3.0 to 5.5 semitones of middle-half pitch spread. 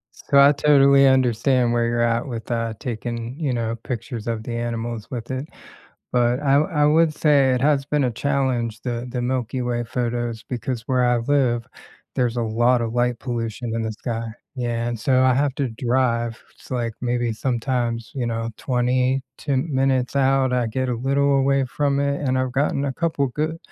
No: narrow, 2.4 semitones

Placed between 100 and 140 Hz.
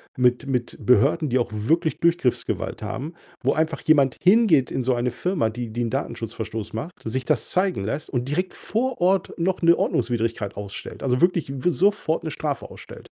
Yes: low, 135 Hz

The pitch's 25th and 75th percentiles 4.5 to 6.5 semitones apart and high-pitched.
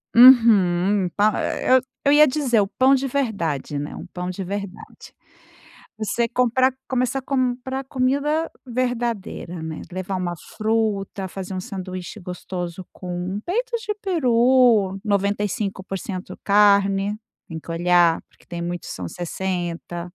Yes: wide, 5.6 semitones; high, 200 Hz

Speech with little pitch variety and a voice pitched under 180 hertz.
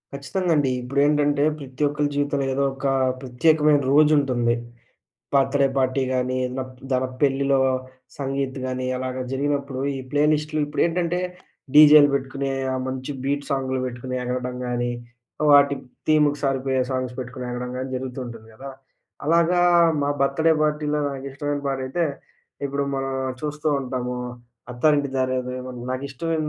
Yes: narrow, 2.2 semitones; low, 135 Hz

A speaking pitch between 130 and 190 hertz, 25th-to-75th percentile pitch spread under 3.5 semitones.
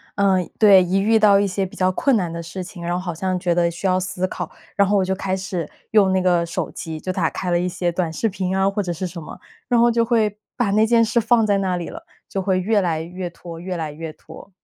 Yes: medium, 185 Hz; narrow, 2.5 semitones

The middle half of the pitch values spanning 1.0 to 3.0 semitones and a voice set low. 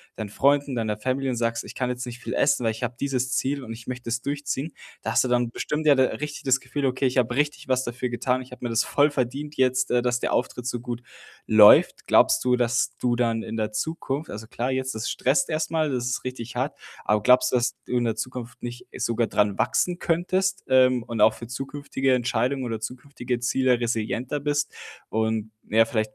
Yes: narrow, 2.5 semitones; low, 125 Hz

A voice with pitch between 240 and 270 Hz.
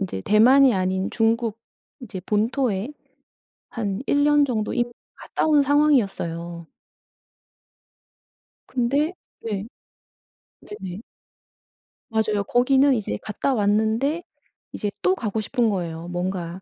No: high, 220 Hz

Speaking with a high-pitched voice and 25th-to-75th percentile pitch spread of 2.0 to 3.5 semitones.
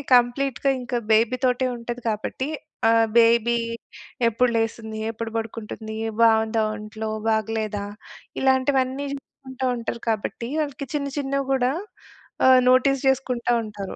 Yes: high, 240 Hz; average, 2.9 semitones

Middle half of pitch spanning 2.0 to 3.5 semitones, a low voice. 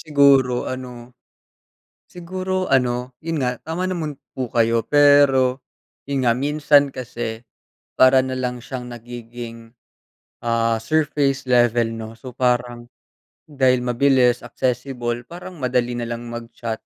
Yes: average, 2.7 semitones; low, 125 Hz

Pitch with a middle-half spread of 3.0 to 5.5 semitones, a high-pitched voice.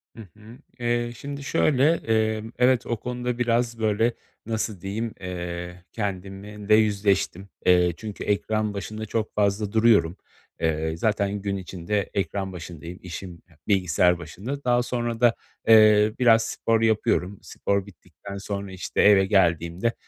No: average, 3.3 semitones; low, 105 Hz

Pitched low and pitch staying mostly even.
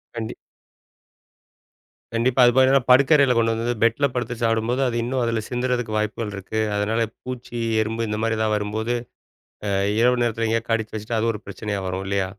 Yes: low, 115 Hz; narrow, 2.1 semitones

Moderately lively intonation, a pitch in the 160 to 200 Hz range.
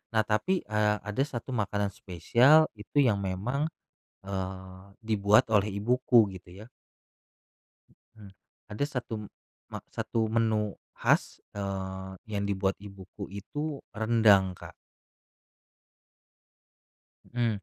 No: average, 3.0 semitones; low, 105 Hz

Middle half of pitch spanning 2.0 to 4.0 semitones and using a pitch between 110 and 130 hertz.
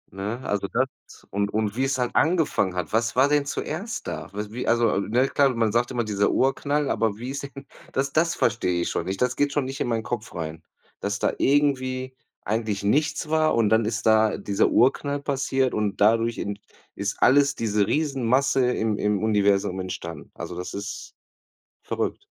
No: average, 4.8 semitones; low, 115 Hz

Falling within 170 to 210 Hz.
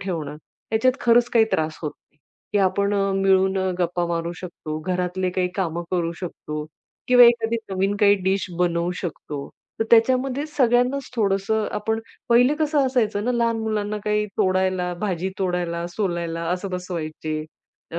Yes: high, 190 Hz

